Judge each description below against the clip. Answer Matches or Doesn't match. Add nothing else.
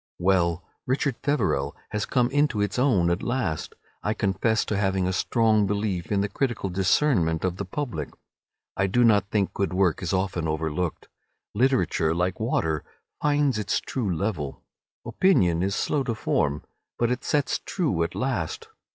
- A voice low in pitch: Matches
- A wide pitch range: Matches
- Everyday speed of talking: Matches